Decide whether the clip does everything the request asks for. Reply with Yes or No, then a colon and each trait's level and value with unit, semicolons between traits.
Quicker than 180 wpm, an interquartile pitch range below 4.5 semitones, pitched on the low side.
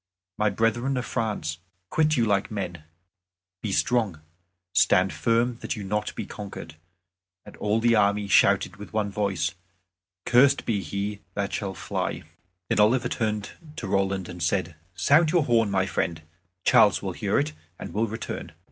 No: average, 160 wpm; average, 3.1 semitones; low, 105 Hz